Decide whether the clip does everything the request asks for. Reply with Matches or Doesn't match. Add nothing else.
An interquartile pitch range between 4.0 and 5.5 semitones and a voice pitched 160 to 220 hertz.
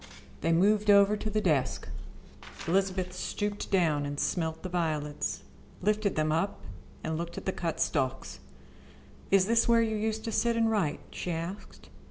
Matches